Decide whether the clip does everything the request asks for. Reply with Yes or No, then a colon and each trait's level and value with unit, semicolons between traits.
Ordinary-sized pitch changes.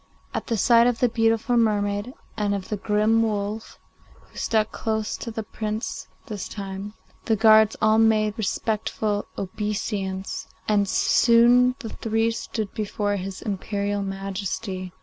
No: narrow, 1.8 semitones